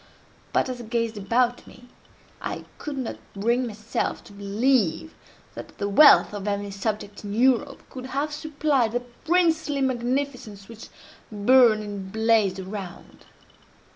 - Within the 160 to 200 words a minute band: No, average, 140 wpm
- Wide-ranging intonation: No, average, 4.4 semitones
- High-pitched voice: Yes, high, 230 Hz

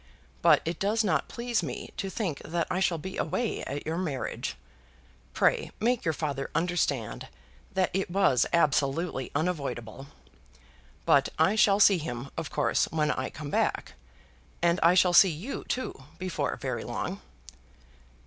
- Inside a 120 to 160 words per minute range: Yes, average, 150 wpm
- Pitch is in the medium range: Yes, medium, 170 Hz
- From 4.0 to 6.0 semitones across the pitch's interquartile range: Yes, average, 4.8 semitones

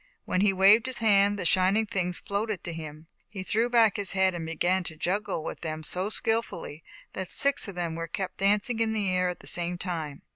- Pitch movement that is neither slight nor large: Yes, average, 3.2 semitones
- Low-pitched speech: No, high, 190 Hz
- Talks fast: Yes, fast, 220 wpm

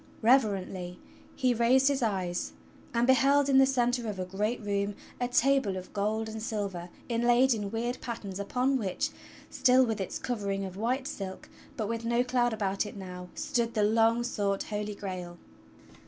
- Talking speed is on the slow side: No, average, 170 wpm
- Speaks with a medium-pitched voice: No, high, 220 Hz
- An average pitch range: Yes, average, 3.7 semitones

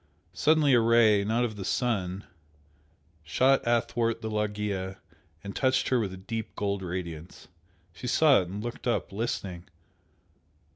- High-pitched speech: No, low, 105 Hz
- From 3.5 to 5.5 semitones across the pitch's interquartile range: Yes, average, 3.9 semitones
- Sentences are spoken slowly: No, average, 145 wpm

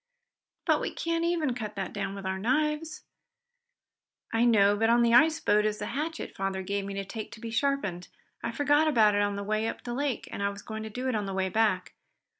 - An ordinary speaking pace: No, fast, 235 wpm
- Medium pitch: No, high, 220 Hz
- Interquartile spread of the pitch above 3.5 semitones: Yes, average, 4.5 semitones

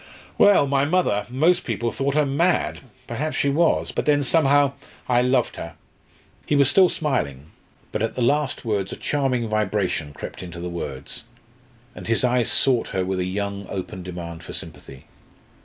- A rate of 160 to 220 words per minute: Yes, average, 175 wpm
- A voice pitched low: Yes, low, 120 Hz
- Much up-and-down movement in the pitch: Yes, wide, 7.3 semitones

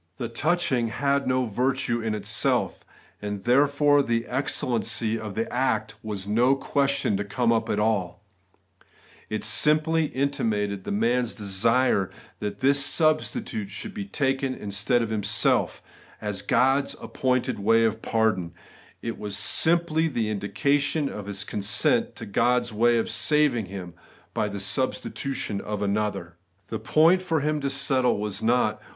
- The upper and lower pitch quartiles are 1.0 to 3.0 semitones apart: No, average, 4.9 semitones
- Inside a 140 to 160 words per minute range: Yes, average, 145 wpm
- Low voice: Yes, low, 115 Hz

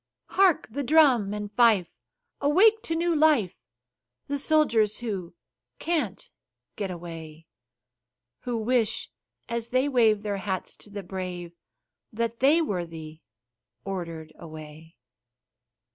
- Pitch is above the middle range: Yes, high, 215 Hz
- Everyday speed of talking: No, slow, 115 wpm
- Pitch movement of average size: No, wide, 7.6 semitones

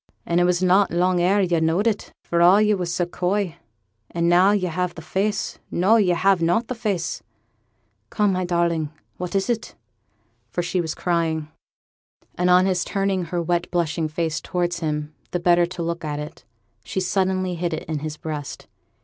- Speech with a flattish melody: Yes, narrow, 2.0 semitones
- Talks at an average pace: Yes, average, 190 wpm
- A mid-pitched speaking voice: Yes, medium, 175 Hz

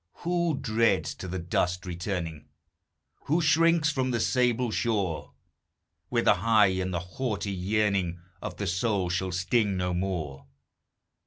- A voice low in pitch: Yes, low, 100 Hz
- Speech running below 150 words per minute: Yes, slow, 135 wpm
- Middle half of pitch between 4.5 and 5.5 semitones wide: Yes, average, 5.0 semitones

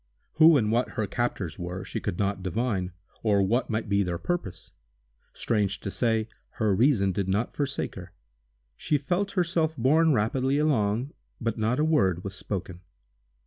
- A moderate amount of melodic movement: No, wide, 6.0 semitones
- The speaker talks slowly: No, average, 165 wpm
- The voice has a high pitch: No, low, 110 Hz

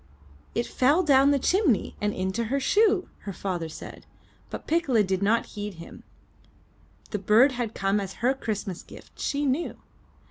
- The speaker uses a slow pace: No, average, 165 wpm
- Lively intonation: Yes, wide, 5.9 semitones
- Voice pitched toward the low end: No, high, 230 Hz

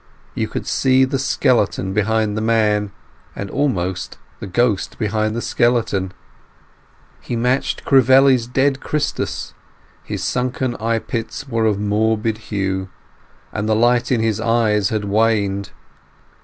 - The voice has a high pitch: No, low, 110 Hz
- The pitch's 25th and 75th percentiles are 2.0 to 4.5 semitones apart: Yes, average, 3.0 semitones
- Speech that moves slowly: Yes, slow, 130 wpm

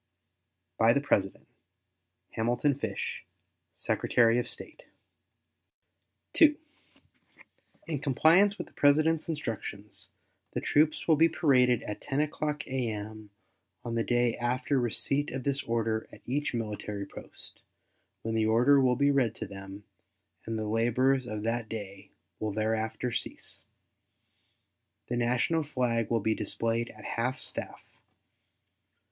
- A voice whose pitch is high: No, low, 120 Hz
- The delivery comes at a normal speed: No, slow, 130 wpm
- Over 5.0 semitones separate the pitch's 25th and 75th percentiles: No, average, 4.2 semitones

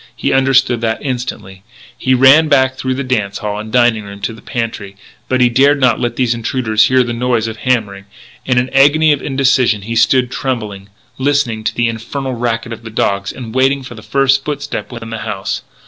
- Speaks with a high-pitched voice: No, low, 120 Hz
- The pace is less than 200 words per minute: No, fast, 205 wpm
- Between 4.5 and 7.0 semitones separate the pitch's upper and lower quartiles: No, average, 2.9 semitones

